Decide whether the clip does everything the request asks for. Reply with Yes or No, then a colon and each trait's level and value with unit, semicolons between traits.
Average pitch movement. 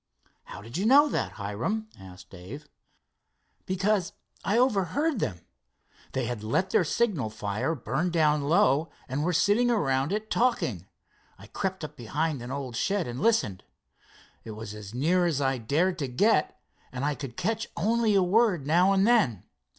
No: wide, 8.5 semitones